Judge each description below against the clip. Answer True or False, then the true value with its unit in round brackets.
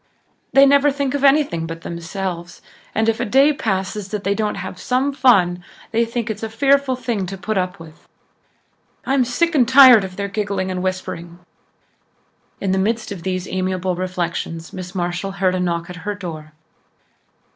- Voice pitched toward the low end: False (195 Hz)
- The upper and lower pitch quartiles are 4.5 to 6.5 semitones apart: True (4.9 semitones)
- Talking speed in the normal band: True (180 wpm)